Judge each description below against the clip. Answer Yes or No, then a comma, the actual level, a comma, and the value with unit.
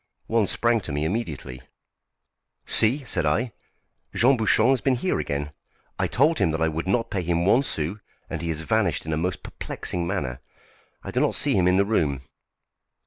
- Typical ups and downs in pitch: No, wide, 6.6 semitones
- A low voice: Yes, very low, 90 Hz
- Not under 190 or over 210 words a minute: Yes, average, 195 wpm